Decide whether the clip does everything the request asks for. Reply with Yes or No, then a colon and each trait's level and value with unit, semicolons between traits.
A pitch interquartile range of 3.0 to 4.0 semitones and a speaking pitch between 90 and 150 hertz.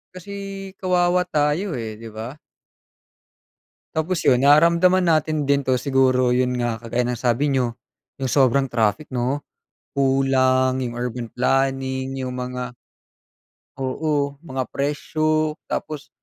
Yes: average, 3.3 semitones; low, 135 Hz